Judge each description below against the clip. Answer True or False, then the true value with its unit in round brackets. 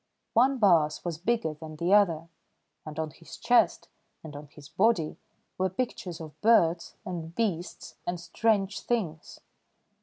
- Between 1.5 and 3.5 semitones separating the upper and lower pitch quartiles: False (4.6 semitones)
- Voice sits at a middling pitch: True (170 Hz)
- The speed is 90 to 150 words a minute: True (145 wpm)